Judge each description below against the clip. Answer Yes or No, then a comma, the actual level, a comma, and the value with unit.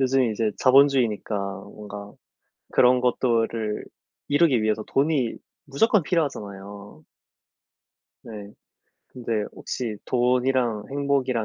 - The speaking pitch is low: Yes, low, 120 Hz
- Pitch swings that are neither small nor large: Yes, average, 4.1 semitones